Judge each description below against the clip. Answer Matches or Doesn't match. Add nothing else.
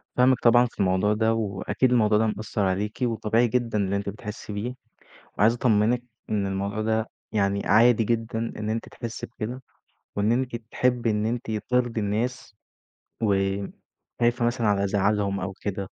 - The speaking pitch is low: Matches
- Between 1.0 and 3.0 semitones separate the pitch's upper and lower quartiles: Matches